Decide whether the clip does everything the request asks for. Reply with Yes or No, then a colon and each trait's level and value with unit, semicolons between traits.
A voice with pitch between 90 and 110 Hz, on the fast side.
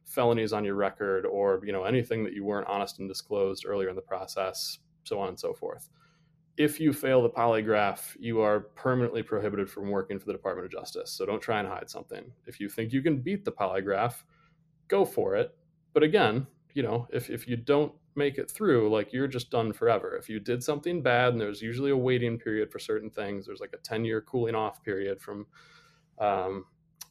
No: low, 120 Hz; fast, 210 wpm